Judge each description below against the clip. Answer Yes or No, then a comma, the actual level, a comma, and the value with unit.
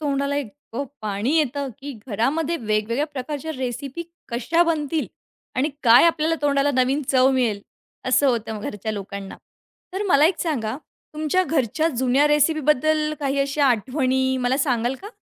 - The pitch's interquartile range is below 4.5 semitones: Yes, average, 3.6 semitones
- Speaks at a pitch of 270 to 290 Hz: Yes, very high, 275 Hz